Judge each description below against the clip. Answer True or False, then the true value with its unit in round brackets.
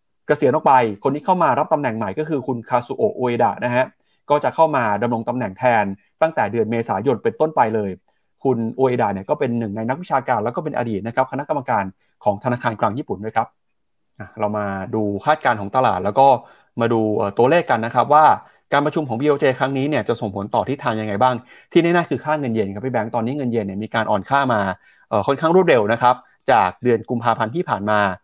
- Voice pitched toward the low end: True (120 Hz)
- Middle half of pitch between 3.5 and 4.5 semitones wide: True (4.0 semitones)